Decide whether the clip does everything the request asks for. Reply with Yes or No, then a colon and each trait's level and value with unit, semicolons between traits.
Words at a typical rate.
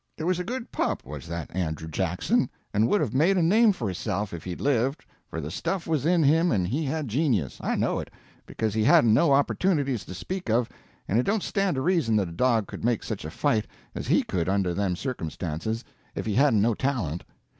No: fast, 225 wpm